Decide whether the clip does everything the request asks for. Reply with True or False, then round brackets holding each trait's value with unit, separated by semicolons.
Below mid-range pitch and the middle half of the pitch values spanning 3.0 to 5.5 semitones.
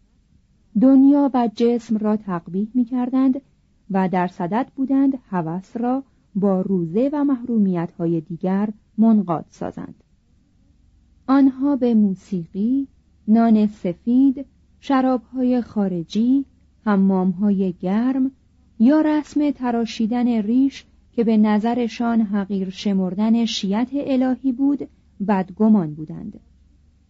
False (220 Hz; 5.2 semitones)